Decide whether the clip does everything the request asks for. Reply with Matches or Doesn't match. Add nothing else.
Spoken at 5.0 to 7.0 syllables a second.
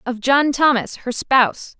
Doesn't match